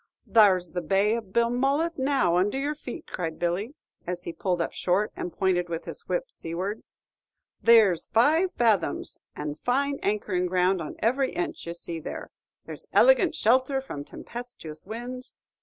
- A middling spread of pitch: No, wide, 6.4 semitones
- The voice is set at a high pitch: Yes, high, 210 Hz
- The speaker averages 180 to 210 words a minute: No, average, 155 wpm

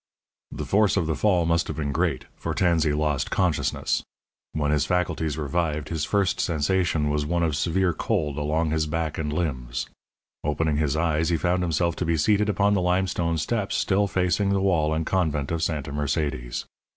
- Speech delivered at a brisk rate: No, average, 185 wpm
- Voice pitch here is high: No, very low, 80 Hz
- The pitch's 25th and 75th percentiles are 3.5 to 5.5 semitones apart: No, average, 3.1 semitones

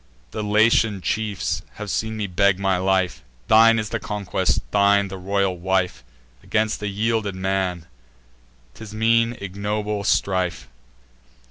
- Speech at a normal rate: No, slow, 130 wpm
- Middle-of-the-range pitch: No, low, 100 Hz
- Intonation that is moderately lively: No, narrow, 2.3 semitones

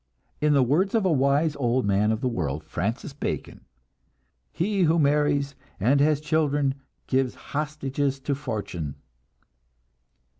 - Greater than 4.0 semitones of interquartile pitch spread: No, average, 3.5 semitones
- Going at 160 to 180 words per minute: No, slow, 135 wpm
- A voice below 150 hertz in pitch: Yes, medium, 140 Hz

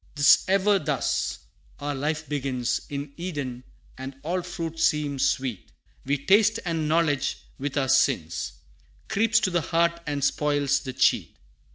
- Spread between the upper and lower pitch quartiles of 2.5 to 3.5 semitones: No, average, 3.9 semitones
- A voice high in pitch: No, medium, 145 Hz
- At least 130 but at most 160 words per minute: Yes, average, 145 wpm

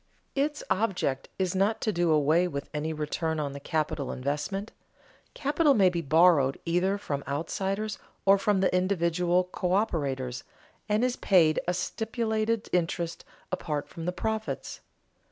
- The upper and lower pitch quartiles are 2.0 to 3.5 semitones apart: No, average, 4.9 semitones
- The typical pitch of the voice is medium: Yes, medium, 180 Hz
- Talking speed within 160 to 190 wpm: No, average, 145 wpm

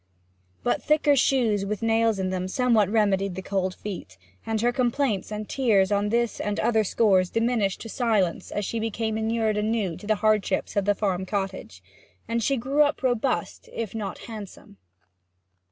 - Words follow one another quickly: No, average, 170 wpm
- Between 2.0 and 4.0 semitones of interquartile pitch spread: Yes, average, 2.9 semitones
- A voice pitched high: Yes, high, 215 Hz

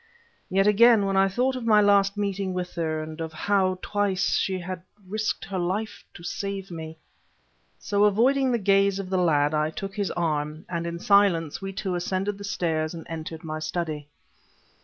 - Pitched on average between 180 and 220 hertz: Yes, high, 190 Hz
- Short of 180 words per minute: No, average, 185 wpm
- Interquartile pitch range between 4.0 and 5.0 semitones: No, average, 3.5 semitones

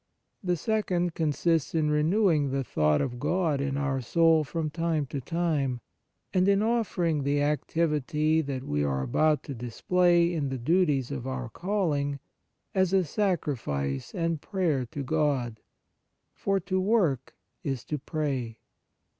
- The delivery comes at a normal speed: Yes, average, 150 wpm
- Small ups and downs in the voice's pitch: No, average, 4.3 semitones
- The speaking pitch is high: No, medium, 150 Hz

